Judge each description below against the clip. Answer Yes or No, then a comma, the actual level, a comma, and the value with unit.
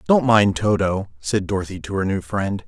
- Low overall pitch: Yes, low, 100 Hz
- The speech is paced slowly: No, average, 200 wpm